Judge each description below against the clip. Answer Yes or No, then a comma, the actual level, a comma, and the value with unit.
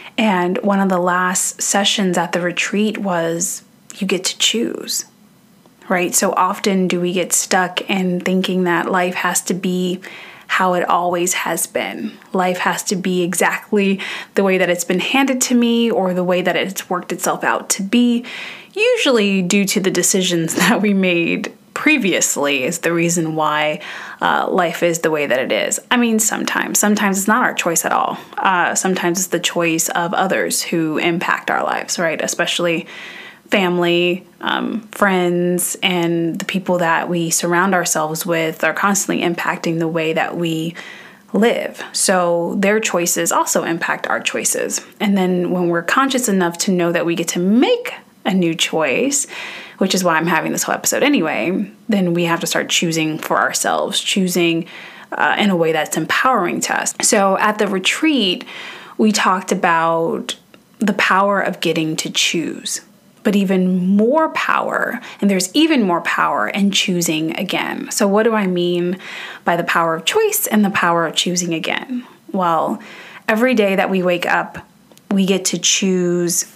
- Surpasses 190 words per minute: No, average, 170 wpm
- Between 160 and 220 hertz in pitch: Yes, medium, 185 Hz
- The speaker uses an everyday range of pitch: Yes, average, 3.1 semitones